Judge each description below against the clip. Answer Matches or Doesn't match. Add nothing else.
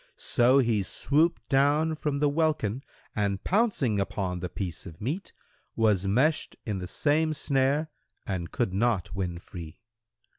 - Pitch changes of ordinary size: Doesn't match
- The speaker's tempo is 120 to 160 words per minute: Matches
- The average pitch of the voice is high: Doesn't match